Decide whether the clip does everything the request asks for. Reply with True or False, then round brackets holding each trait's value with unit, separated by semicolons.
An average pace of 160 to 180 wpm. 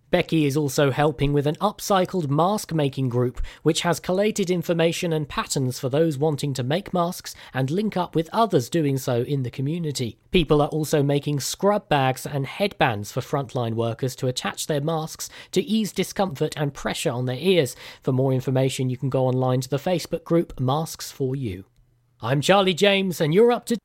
False (190 wpm)